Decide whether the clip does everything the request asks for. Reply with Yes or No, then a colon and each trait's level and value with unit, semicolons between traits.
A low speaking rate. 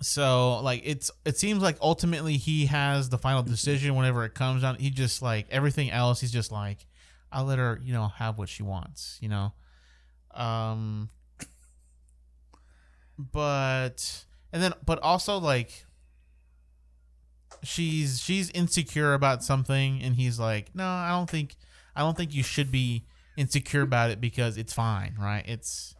No: average, 155 wpm